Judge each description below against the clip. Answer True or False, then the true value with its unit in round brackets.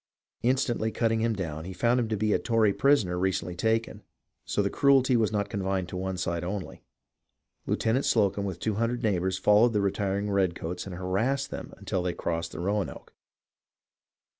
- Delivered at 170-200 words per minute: True (180 wpm)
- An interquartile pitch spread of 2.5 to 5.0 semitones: True (3.5 semitones)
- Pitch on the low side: True (100 Hz)